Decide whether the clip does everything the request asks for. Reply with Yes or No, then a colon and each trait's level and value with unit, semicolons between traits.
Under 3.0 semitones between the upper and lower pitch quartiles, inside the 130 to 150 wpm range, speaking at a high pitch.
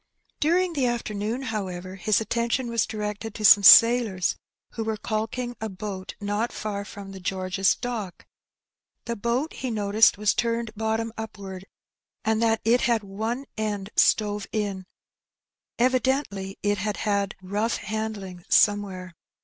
Yes: narrow, 2.6 semitones; average, 140 wpm; high, 215 Hz